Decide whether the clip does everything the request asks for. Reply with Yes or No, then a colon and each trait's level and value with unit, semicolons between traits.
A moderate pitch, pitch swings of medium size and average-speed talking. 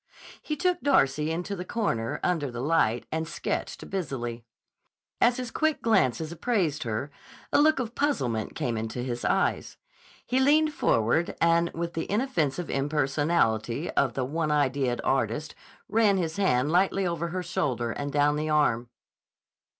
No: medium, 155 Hz; wide, 7.0 semitones; average, 150 wpm